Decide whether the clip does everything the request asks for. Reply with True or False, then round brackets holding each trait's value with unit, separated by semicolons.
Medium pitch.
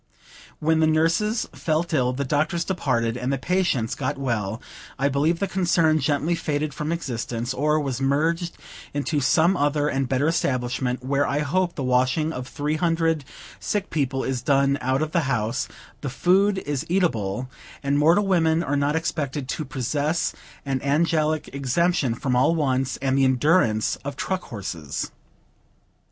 True (145 Hz)